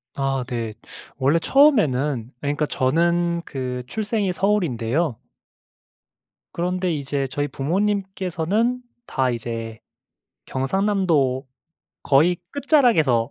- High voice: No, medium, 150 Hz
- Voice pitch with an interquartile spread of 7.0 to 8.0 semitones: No, wide, 6.6 semitones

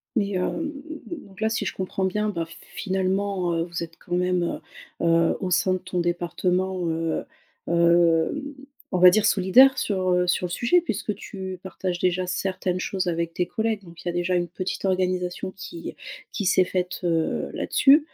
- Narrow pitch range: Yes, narrow, 1.8 semitones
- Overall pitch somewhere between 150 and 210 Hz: Yes, medium, 185 Hz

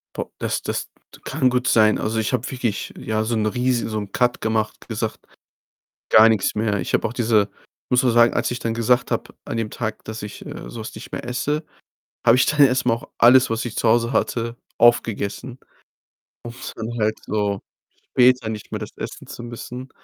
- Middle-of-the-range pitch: No, low, 115 Hz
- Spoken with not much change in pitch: Yes, narrow, 2.2 semitones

